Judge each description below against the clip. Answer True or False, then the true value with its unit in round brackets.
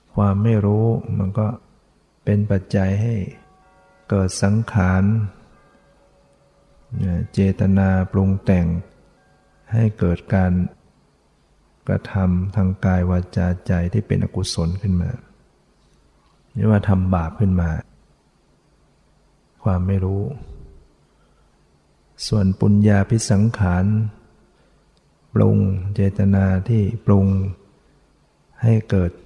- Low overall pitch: True (95 Hz)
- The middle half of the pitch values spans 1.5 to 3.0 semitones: True (2.5 semitones)